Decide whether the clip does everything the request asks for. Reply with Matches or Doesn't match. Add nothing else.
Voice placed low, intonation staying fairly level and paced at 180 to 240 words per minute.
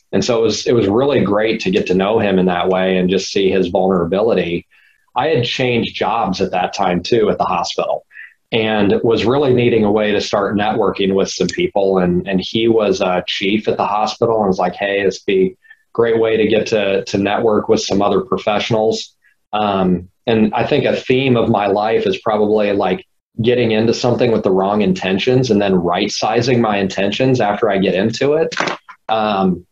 Doesn't match